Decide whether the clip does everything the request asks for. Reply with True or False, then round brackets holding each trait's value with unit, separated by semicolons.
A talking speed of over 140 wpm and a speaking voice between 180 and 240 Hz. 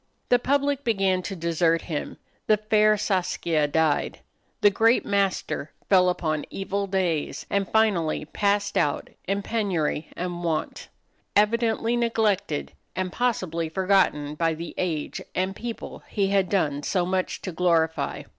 False (135 wpm; 185 Hz)